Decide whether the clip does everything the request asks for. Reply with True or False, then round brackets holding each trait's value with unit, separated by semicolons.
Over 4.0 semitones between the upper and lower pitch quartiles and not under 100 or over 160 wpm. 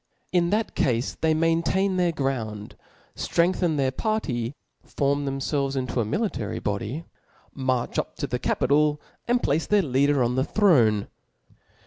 True (5.1 semitones; 140 wpm)